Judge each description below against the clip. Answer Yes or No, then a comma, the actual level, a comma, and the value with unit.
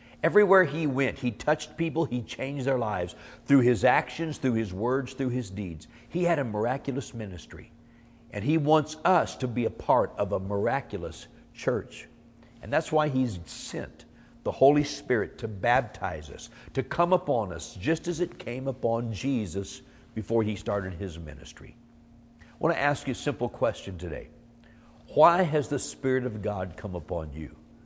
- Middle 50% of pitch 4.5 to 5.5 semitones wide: Yes, average, 4.8 semitones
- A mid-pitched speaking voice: No, low, 120 Hz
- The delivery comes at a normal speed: Yes, average, 170 wpm